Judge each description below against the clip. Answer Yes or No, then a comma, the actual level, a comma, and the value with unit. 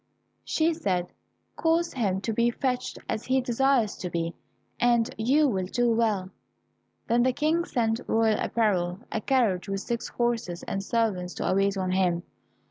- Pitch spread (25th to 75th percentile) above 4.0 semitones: Yes, average, 4.7 semitones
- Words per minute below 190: Yes, average, 160 wpm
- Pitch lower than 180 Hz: No, high, 225 Hz